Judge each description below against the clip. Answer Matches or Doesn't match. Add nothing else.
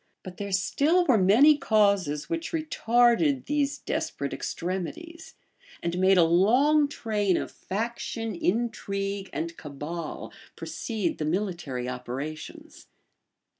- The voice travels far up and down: Matches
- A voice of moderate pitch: Doesn't match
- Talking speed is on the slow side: Matches